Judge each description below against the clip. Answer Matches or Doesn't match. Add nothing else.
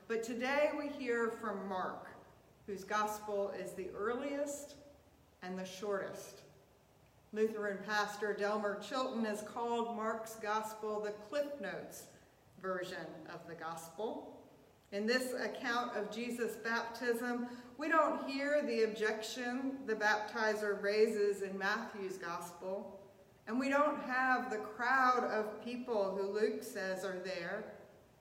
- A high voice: Matches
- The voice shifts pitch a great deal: Doesn't match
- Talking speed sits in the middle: Doesn't match